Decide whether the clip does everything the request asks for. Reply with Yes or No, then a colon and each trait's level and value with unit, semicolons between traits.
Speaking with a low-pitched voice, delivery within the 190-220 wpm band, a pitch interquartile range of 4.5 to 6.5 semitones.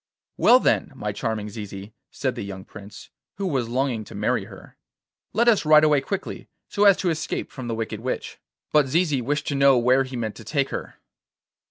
Yes: low, 130 Hz; average, 200 wpm; average, 5.1 semitones